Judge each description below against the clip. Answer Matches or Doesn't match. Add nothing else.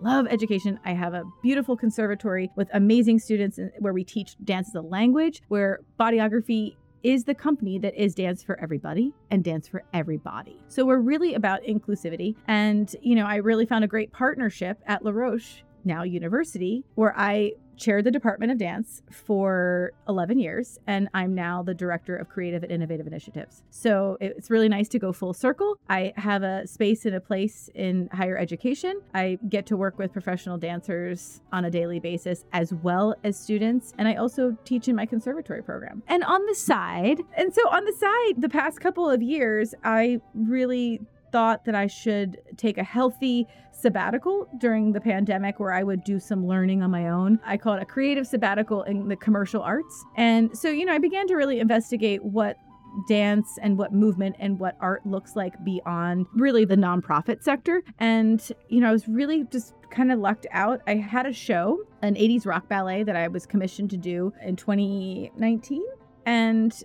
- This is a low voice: Doesn't match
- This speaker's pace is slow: Doesn't match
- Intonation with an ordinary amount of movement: Matches